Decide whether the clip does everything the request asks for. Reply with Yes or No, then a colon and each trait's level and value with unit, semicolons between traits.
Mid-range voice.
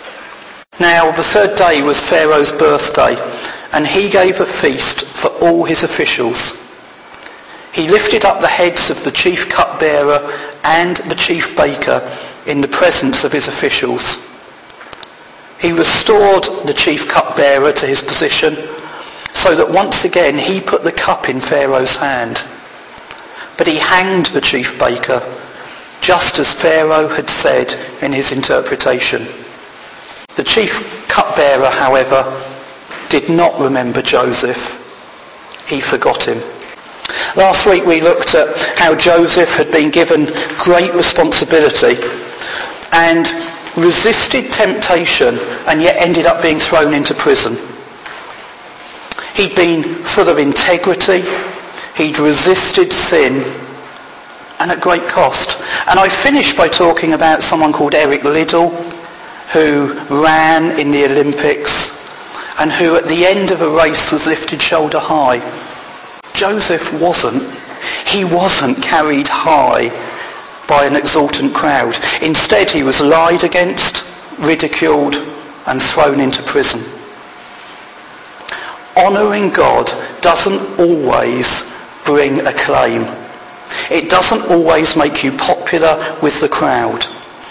Yes: medium, 165 Hz